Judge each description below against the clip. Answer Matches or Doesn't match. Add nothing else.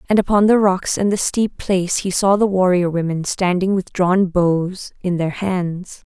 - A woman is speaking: Matches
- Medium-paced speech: Matches